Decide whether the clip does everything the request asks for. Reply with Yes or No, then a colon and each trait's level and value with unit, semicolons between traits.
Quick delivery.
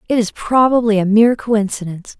No: average, 165 wpm